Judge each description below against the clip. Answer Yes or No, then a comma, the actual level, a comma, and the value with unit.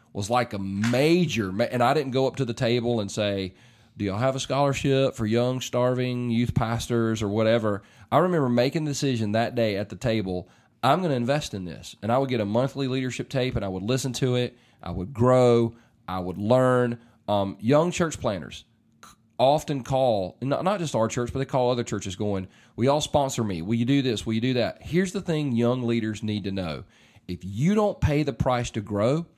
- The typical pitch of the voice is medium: No, low, 120 Hz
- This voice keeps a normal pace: No, fast, 215 wpm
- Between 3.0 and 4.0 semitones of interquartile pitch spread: Yes, average, 3.6 semitones